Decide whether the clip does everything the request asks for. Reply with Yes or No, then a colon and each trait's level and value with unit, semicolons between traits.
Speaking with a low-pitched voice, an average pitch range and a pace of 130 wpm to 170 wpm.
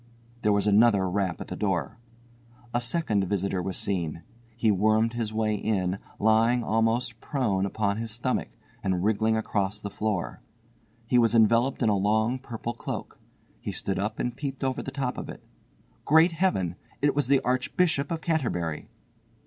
Yes: low, 110 Hz; average, 3.7 semitones; average, 165 wpm